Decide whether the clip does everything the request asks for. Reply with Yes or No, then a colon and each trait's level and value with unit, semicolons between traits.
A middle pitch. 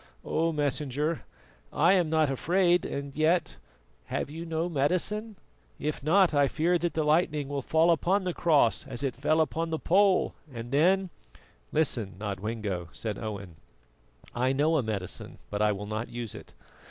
Yes: medium, 150 Hz